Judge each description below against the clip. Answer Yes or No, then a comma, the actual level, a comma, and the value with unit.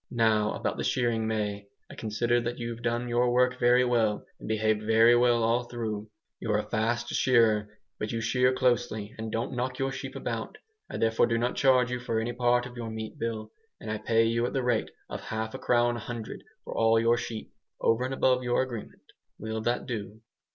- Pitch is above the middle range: No, low, 115 Hz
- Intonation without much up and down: Yes, narrow, 1.7 semitones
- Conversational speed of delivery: No, fast, 210 wpm